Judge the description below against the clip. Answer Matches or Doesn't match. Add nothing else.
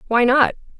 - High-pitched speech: Matches